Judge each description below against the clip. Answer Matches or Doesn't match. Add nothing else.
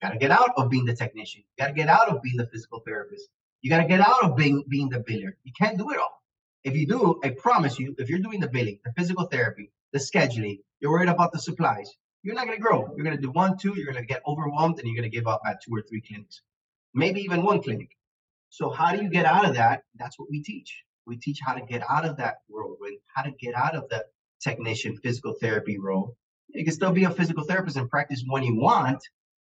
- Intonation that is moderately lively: Doesn't match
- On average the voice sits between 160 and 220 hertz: Doesn't match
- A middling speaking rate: Doesn't match